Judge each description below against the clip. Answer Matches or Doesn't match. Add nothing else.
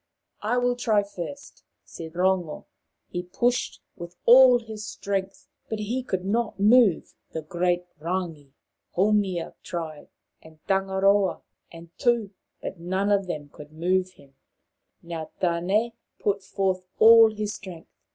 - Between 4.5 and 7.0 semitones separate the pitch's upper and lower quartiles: Doesn't match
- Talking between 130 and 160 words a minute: Matches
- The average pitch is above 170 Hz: Matches